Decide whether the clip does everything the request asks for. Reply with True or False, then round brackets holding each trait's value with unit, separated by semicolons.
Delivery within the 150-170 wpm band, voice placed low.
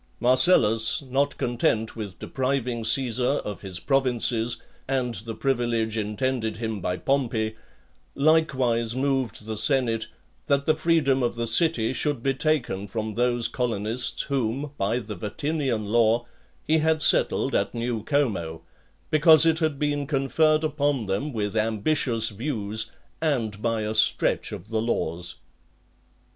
False (135 wpm; 120 Hz)